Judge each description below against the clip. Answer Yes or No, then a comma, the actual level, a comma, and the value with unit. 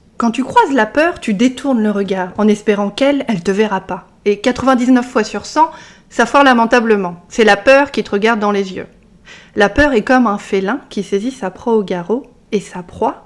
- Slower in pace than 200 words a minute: No, average, 215 wpm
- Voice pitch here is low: No, high, 215 Hz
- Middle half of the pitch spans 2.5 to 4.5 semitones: Yes, average, 4.1 semitones